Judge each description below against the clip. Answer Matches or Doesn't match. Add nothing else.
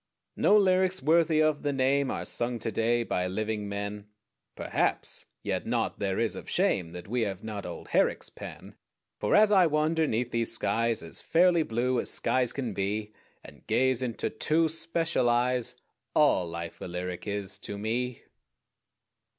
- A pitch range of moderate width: Doesn't match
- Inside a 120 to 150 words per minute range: Doesn't match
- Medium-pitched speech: Doesn't match